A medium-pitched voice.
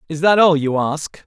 Yes: medium, 160 Hz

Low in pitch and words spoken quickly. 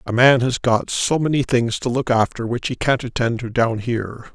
Yes: low, 120 Hz; fast, 235 wpm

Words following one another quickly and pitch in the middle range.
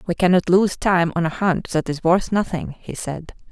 Yes: fast, 220 wpm; medium, 175 Hz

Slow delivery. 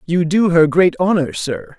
No: average, 200 wpm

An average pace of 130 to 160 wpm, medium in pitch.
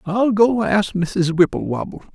Yes: average, 140 wpm; medium, 180 Hz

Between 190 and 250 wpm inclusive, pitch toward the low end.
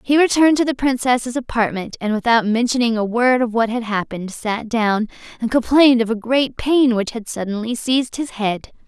No: average, 195 wpm; high, 235 Hz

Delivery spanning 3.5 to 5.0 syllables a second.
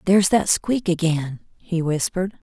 Yes: 4.8 syllables/s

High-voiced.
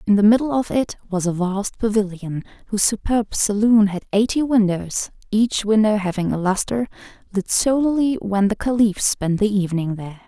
Yes: high, 210 Hz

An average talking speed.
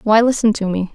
No: fast, 255 wpm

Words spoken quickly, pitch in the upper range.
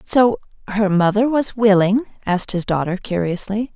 No: average, 145 wpm; high, 205 Hz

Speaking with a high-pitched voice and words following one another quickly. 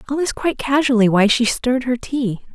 Yes: very high, 250 Hz; fast, 210 wpm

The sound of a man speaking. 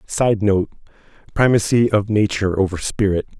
Yes: male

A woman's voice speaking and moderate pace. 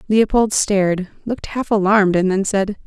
Yes: female; average, 170 wpm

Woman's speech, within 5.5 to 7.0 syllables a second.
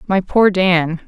No: female; 3.4 syllables/s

